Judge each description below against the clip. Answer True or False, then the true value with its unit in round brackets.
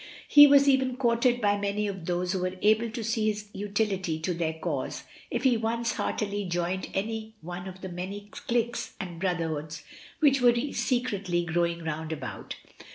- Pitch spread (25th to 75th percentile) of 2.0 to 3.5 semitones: False (4.7 semitones)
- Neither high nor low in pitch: False (200 Hz)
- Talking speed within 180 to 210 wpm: False (170 wpm)